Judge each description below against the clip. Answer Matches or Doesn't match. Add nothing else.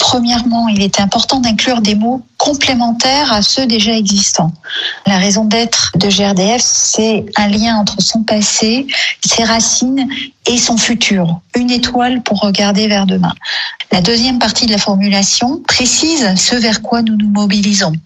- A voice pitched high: Matches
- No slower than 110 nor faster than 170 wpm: Matches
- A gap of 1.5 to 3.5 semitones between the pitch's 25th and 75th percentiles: Matches